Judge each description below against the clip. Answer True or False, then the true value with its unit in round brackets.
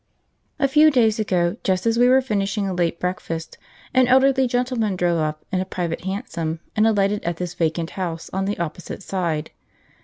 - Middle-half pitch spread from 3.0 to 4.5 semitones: False (4.9 semitones)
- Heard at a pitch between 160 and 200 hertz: True (190 Hz)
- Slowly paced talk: False (185 wpm)